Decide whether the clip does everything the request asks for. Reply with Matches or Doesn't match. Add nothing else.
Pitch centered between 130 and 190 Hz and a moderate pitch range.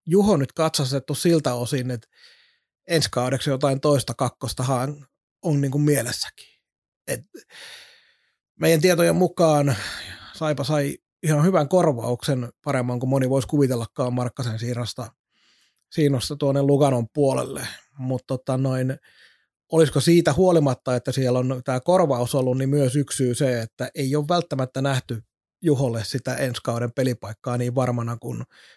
Matches